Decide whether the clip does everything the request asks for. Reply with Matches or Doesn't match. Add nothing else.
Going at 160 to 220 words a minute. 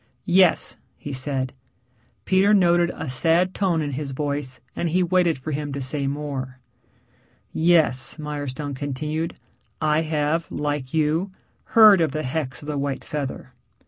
Doesn't match